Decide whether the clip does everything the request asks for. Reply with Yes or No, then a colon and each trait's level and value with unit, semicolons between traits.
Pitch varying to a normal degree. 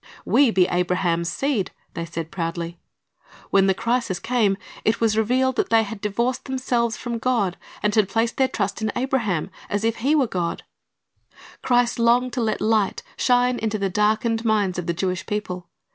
Yes: average, 4.2 semitones